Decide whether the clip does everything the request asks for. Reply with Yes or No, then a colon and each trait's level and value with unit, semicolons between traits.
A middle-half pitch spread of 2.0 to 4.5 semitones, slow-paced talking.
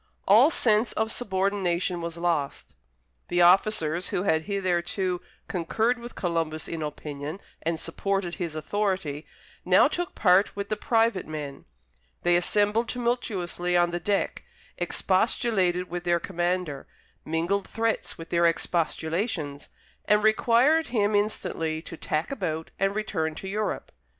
Yes: average, 4.0 semitones; slow, 130 wpm